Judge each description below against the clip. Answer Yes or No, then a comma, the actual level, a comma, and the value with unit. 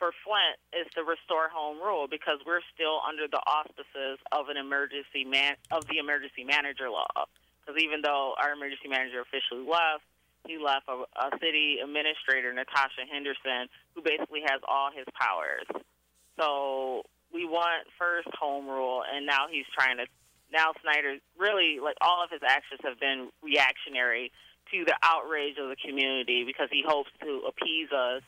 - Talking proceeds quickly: No, average, 165 wpm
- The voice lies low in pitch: No, medium, 145 Hz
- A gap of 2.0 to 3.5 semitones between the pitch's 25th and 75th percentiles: Yes, average, 2.8 semitones